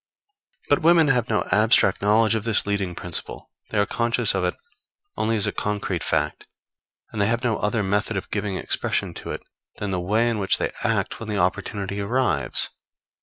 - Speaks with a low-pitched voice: Yes, low, 105 Hz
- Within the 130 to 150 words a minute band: No, average, 190 wpm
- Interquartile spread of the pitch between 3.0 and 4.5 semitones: No, narrow, 2.5 semitones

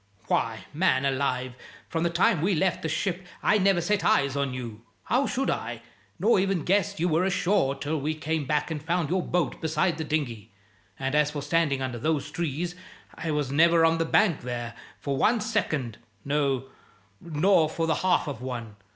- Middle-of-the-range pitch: Yes, medium, 155 Hz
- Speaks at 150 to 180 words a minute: No, average, 190 wpm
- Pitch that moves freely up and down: No, average, 4.4 semitones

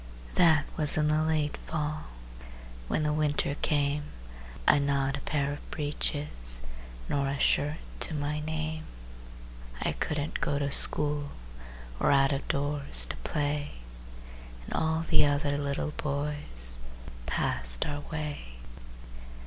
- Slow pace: Yes, slow, 130 wpm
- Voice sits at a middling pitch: Yes, medium, 145 Hz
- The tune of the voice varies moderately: No, narrow, 1.4 semitones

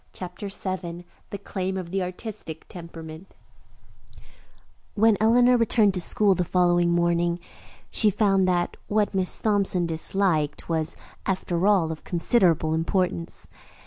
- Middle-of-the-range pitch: Yes, medium, 180 Hz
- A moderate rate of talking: No, slow, 125 wpm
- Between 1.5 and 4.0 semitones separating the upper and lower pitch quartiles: Yes, average, 2.9 semitones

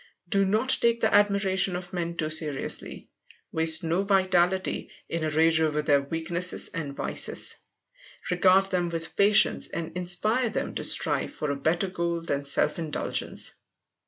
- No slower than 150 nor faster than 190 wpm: Yes, average, 155 wpm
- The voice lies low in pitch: No, medium, 175 Hz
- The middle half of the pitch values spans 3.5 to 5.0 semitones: No, average, 3.0 semitones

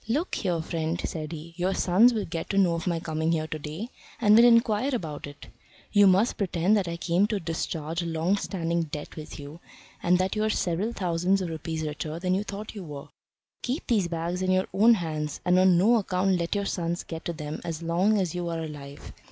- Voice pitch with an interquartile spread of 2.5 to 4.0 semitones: Yes, average, 3.4 semitones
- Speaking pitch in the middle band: Yes, medium, 175 Hz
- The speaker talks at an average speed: No, fast, 225 wpm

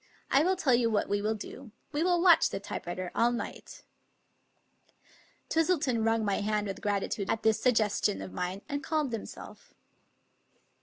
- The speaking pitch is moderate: No, high, 225 Hz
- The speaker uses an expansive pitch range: Yes, wide, 5.8 semitones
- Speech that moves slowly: No, average, 165 wpm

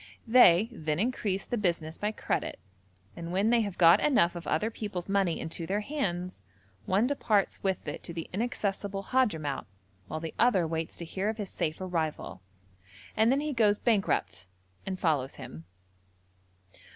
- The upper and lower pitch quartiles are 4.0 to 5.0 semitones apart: Yes, average, 4.6 semitones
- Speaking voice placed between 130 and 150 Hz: No, high, 190 Hz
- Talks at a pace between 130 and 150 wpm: No, average, 165 wpm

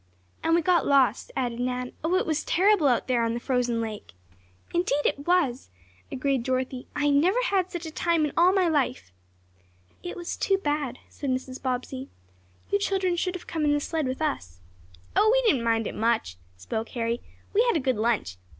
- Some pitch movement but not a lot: No, wide, 5.9 semitones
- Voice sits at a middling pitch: No, very high, 280 Hz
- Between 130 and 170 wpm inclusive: No, average, 195 wpm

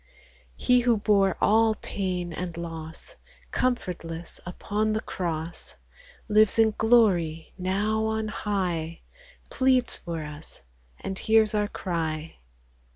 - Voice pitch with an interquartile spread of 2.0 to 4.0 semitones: No, average, 4.5 semitones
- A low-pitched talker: No, high, 195 Hz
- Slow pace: Yes, slow, 110 wpm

